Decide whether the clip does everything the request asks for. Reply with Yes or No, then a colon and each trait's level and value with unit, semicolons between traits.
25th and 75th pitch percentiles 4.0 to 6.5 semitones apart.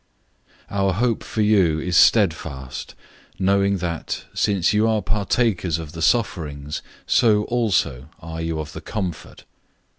Yes: average, 4.7 semitones